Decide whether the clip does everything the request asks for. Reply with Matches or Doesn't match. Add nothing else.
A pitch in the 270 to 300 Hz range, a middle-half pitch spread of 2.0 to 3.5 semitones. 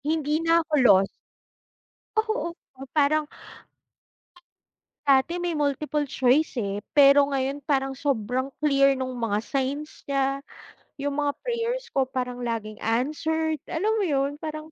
Matches